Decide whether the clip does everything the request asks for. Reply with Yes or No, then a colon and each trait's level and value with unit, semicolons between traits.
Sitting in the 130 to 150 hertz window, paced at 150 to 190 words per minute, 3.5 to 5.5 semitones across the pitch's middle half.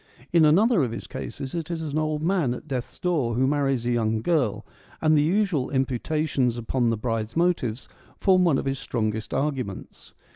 Yes: low, 135 Hz; average, 185 wpm; average, 4.9 semitones